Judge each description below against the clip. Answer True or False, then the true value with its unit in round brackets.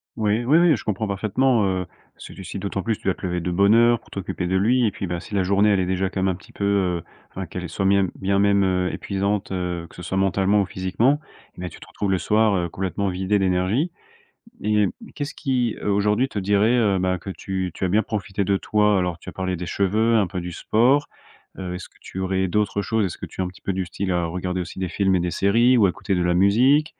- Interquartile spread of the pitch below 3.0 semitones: True (2.4 semitones)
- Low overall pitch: True (95 Hz)